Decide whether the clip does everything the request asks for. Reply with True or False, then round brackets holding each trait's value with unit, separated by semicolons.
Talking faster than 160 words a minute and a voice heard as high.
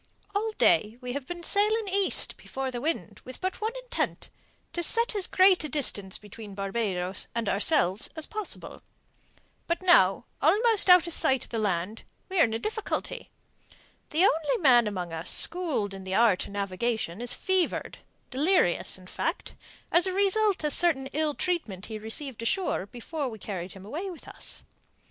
True (170 wpm; 270 Hz)